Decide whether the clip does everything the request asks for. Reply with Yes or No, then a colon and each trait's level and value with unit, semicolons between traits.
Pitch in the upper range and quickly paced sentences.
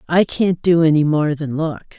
No: medium, 160 Hz; fast, 210 wpm